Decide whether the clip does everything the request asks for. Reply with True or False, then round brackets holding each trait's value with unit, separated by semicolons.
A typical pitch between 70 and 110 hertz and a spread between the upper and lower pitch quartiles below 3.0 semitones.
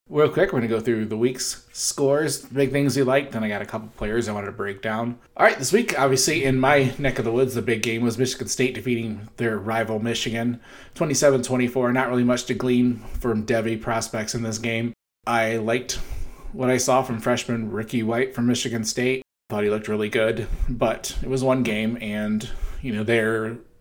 False (120 Hz; 2.4 semitones)